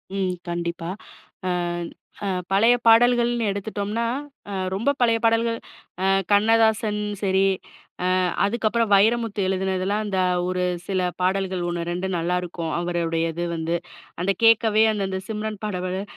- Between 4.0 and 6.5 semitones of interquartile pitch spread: No, average, 3.5 semitones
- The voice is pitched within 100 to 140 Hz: No, high, 195 Hz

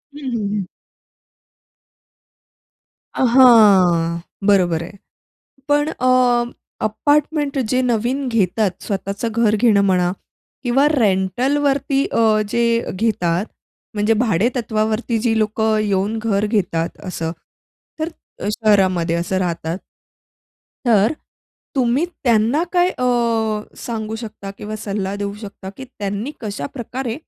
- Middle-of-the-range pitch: No, high, 215 Hz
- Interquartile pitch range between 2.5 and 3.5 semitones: No, average, 4.0 semitones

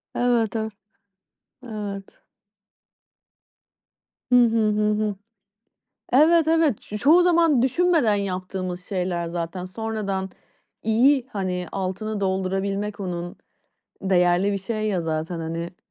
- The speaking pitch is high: Yes, high, 200 Hz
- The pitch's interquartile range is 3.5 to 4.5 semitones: Yes, average, 3.8 semitones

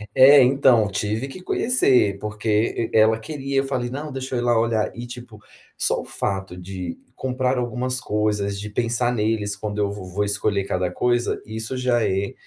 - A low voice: Yes, low, 115 Hz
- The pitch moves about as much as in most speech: Yes, average, 3.6 semitones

